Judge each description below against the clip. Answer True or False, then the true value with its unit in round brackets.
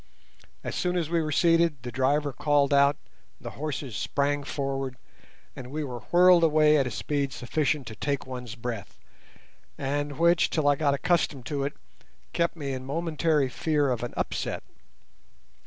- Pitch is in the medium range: True (145 Hz)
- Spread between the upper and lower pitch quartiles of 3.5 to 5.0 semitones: False (2.8 semitones)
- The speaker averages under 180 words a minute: True (165 wpm)